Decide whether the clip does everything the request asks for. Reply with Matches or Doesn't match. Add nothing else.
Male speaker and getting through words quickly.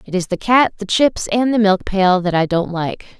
Doesn't match